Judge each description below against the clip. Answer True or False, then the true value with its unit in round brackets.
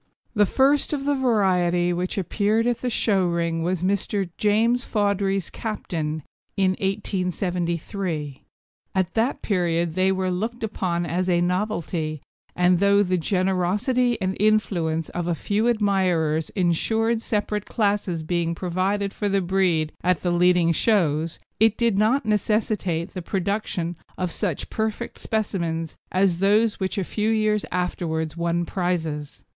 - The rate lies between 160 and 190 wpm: False (140 wpm)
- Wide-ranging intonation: False (3.5 semitones)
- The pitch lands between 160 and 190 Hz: True (185 Hz)